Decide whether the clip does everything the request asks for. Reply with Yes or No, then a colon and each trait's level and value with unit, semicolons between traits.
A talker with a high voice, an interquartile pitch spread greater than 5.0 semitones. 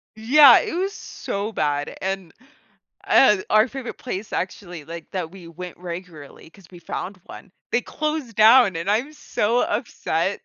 Yes: high, 195 Hz; wide, 5.6 semitones